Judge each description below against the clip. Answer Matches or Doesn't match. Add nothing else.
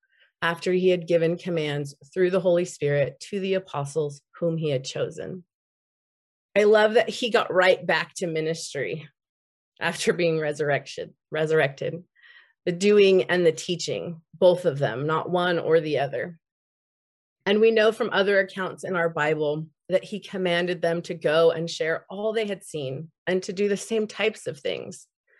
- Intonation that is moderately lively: Matches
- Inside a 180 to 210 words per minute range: Doesn't match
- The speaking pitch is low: Doesn't match